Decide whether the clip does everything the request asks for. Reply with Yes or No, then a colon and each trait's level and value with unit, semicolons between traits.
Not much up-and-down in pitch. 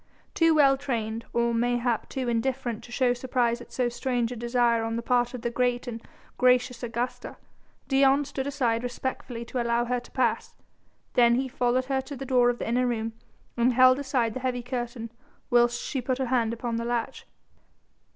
Yes: narrow, 1.5 semitones